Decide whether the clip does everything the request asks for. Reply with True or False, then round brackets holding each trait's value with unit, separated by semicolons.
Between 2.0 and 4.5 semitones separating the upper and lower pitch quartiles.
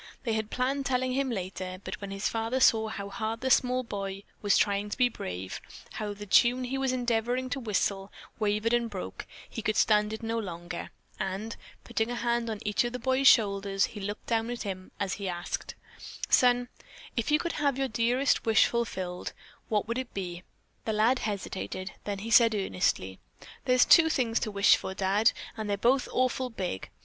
True (3.6 semitones)